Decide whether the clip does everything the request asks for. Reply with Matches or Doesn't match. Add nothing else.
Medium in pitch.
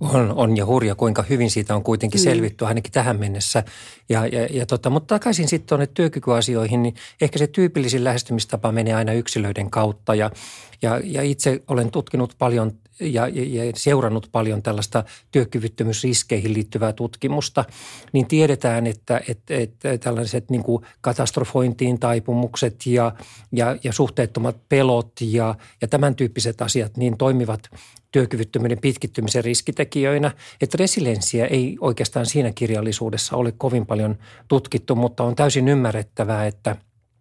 Doesn't match